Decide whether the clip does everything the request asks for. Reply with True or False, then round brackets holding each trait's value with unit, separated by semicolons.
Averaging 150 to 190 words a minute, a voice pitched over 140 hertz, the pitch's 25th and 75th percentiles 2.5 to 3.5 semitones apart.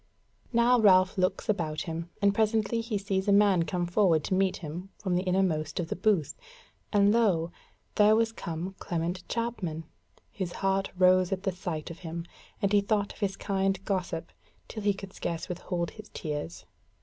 True (180 wpm; 190 Hz; 3.1 semitones)